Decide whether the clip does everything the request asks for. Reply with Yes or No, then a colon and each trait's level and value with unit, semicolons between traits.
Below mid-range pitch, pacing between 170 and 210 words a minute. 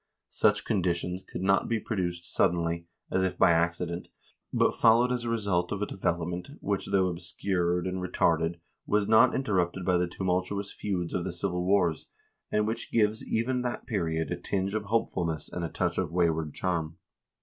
Yes: very low, 90 Hz; average, 175 wpm